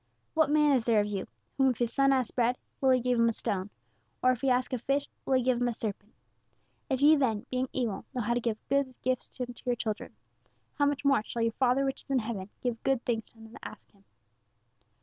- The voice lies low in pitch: No, very high, 250 Hz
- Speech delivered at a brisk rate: Yes, fast, 250 wpm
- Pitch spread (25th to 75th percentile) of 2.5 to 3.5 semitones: Yes, average, 2.8 semitones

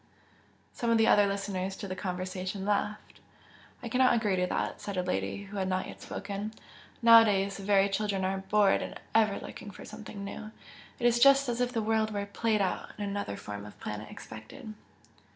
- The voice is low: No, high, 200 Hz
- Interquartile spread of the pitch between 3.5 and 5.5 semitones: No, narrow, 2.4 semitones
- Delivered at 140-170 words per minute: No, average, 200 wpm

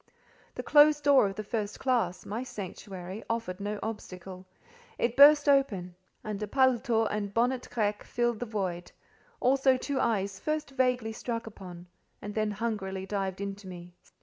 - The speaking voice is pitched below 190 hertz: No, high, 215 Hz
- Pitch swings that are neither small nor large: Yes, average, 4.3 semitones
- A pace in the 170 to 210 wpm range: No, average, 150 wpm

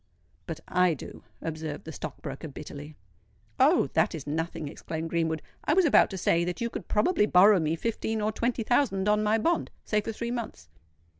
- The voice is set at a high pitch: No, medium, 180 Hz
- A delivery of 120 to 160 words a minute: No, average, 190 wpm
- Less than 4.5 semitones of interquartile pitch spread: No, wide, 5.6 semitones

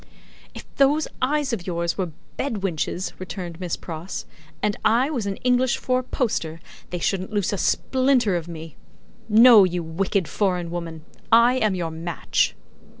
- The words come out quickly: No, average, 155 wpm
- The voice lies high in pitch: Yes, high, 195 Hz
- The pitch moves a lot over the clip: Yes, wide, 6.1 semitones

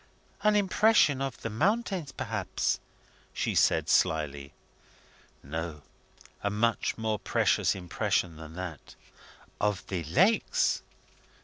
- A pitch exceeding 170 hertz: No, low, 105 Hz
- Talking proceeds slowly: Yes, slow, 105 wpm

